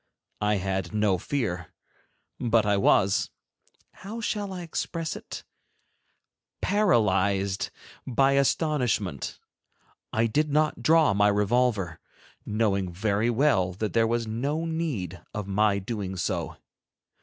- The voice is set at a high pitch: No, low, 110 Hz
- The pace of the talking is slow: Yes, slow, 110 wpm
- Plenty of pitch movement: Yes, wide, 6.4 semitones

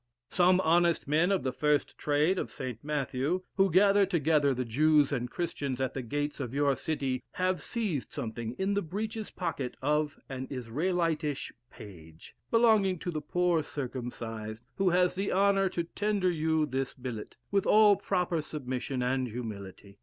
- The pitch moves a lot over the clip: Yes, wide, 6.0 semitones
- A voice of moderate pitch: Yes, medium, 150 Hz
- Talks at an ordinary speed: Yes, average, 160 wpm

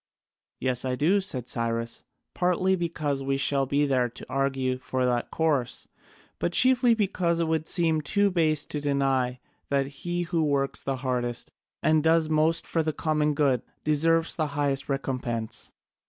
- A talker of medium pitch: Yes, medium, 145 Hz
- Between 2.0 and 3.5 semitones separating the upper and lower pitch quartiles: No, average, 4.0 semitones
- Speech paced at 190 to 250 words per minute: No, average, 160 wpm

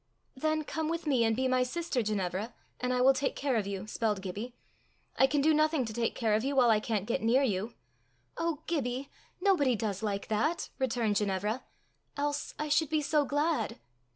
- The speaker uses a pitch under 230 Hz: No, very high, 250 Hz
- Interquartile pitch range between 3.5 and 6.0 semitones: Yes, average, 5.2 semitones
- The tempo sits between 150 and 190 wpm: No, fast, 205 wpm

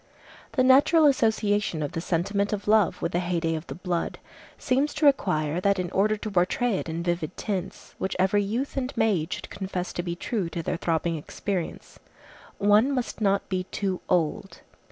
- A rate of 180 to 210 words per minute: Yes, average, 185 wpm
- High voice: Yes, high, 195 Hz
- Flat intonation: No, average, 3.8 semitones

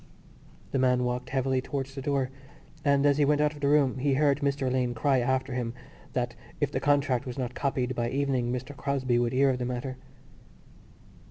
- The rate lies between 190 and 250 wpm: Yes, average, 200 wpm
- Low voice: Yes, low, 130 Hz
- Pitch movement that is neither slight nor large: No, narrow, 2.0 semitones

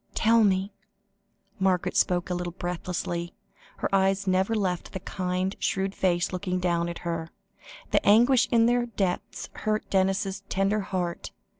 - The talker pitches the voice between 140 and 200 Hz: Yes, high, 190 Hz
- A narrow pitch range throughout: Yes, narrow, 2.1 semitones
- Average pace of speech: Yes, average, 145 wpm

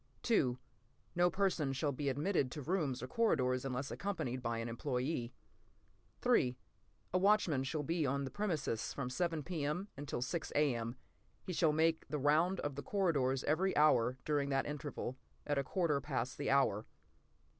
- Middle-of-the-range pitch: Yes, medium, 145 Hz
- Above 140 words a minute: Yes, average, 160 wpm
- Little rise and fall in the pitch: No, average, 4.4 semitones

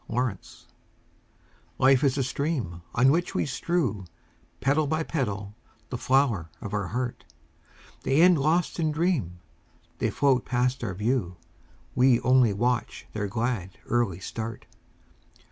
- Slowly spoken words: Yes, slow, 130 wpm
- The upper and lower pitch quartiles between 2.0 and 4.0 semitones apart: No, average, 5.0 semitones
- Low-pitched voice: Yes, low, 125 Hz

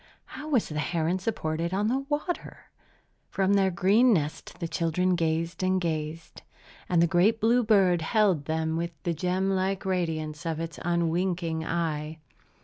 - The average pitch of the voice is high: No, medium, 175 Hz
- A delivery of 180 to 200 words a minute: No, average, 155 wpm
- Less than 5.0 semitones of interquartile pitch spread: Yes, average, 3.0 semitones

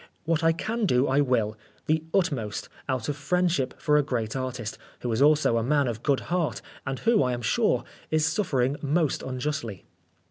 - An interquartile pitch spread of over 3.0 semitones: Yes, average, 4.1 semitones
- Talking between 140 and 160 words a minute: No, average, 185 wpm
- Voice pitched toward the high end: No, medium, 140 Hz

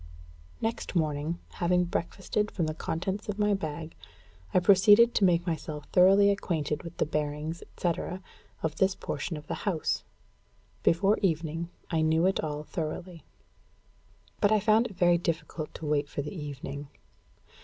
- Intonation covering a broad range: No, average, 3.8 semitones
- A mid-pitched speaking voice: Yes, medium, 170 Hz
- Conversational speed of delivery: Yes, average, 155 wpm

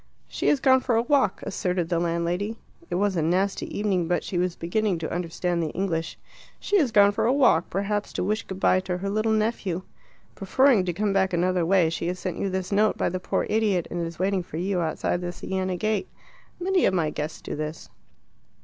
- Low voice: No, medium, 185 Hz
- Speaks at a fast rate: Yes, fast, 220 wpm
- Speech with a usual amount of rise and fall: Yes, average, 3.2 semitones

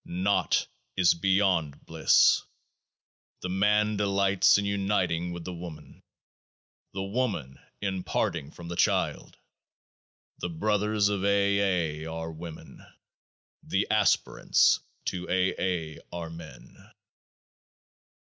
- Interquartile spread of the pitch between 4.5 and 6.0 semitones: No, average, 3.1 semitones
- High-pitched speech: No, very low, 90 Hz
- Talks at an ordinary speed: No, slow, 110 wpm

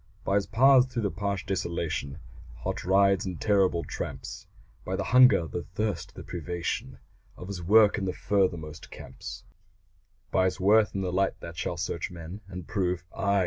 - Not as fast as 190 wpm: Yes, average, 180 wpm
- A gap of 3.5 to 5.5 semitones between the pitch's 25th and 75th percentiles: No, average, 2.7 semitones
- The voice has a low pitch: Yes, very low, 95 Hz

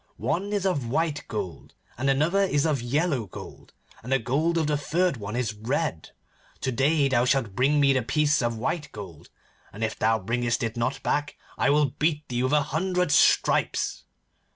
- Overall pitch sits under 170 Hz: Yes, low, 135 Hz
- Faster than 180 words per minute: Yes, average, 190 wpm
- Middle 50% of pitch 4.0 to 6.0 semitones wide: Yes, average, 4.4 semitones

